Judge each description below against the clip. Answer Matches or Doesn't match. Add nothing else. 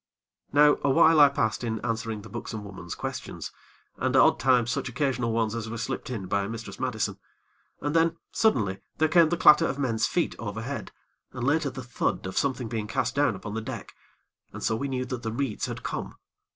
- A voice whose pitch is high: Doesn't match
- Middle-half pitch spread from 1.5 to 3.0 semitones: Doesn't match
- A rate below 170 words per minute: Doesn't match